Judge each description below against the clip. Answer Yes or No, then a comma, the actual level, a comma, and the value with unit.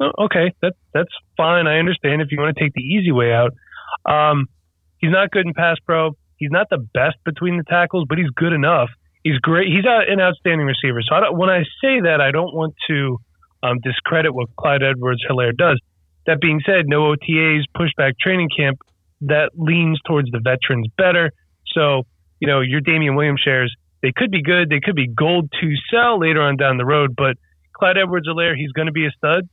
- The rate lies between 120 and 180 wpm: No, fast, 205 wpm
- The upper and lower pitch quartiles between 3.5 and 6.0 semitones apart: Yes, average, 4.2 semitones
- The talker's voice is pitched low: No, medium, 150 Hz